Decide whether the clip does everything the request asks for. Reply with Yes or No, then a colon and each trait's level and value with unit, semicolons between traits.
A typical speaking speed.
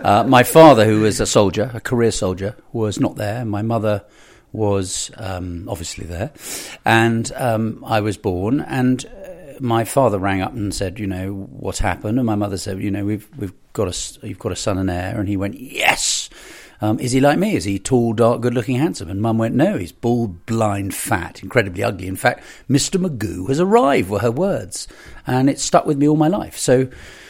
No: fast, 210 wpm